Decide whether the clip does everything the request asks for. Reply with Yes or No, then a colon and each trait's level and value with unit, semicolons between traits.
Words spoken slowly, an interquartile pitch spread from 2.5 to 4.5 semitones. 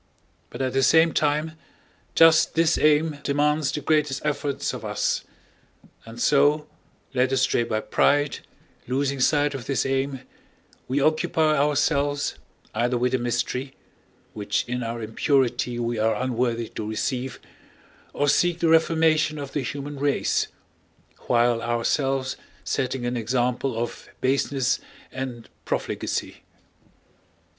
Yes: slow, 125 wpm; average, 3.2 semitones